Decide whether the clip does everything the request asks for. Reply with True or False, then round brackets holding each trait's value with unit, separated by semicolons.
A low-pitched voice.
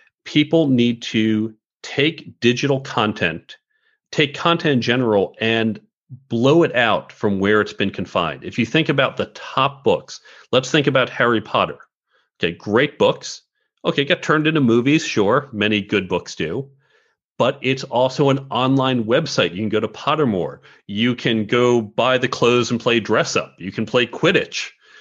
True (125 Hz)